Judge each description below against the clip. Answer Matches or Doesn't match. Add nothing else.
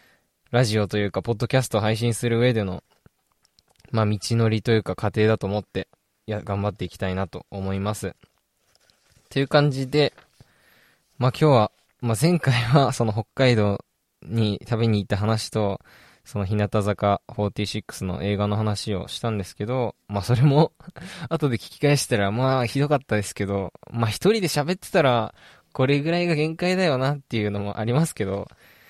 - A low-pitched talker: Matches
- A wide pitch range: Doesn't match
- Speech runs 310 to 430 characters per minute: Matches